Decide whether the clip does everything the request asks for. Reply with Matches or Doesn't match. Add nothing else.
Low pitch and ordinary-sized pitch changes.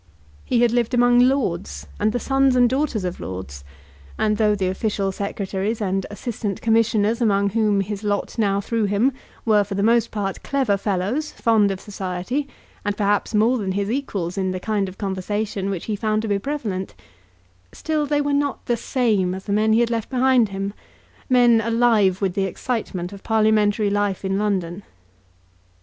Doesn't match